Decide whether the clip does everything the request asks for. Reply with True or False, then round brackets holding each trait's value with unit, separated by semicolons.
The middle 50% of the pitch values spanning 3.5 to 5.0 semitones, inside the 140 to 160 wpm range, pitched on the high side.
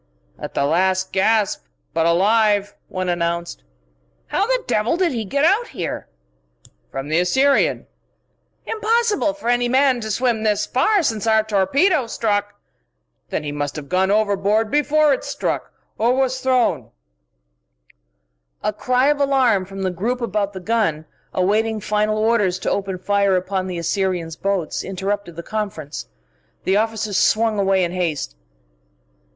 True (4.6 semitones; 155 wpm; 205 Hz)